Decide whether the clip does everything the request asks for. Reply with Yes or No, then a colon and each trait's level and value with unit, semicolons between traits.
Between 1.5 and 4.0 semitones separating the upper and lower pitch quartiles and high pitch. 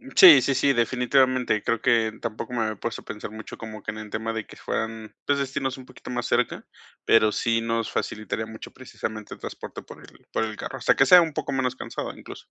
No: average, 2.8 semitones; low, 115 Hz